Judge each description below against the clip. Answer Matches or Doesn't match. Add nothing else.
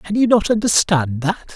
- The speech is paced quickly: Doesn't match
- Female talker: Doesn't match